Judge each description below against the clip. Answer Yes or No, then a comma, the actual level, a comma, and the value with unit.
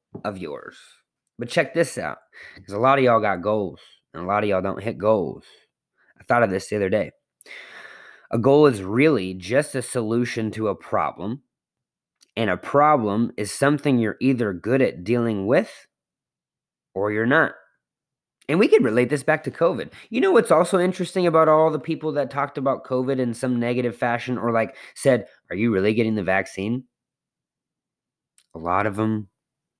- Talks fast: No, average, 180 wpm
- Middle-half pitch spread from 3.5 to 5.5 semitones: Yes, average, 4.7 semitones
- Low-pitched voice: Yes, low, 125 Hz